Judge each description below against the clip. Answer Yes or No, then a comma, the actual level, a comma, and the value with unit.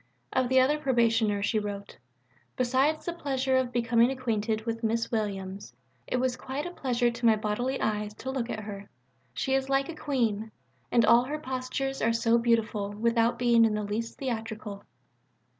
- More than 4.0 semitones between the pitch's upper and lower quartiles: No, average, 3.2 semitones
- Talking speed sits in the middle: Yes, average, 175 wpm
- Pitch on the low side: No, high, 235 Hz